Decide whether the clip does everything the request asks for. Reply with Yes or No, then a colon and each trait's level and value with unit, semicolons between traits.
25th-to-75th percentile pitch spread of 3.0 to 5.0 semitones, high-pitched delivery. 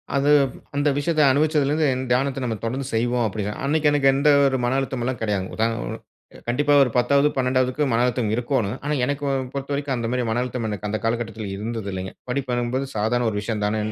No: average, 3.8 semitones; low, 125 Hz